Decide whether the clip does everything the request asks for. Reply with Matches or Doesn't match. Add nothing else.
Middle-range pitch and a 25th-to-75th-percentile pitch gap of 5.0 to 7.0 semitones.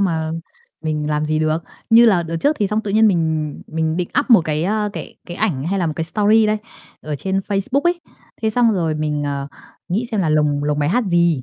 Matches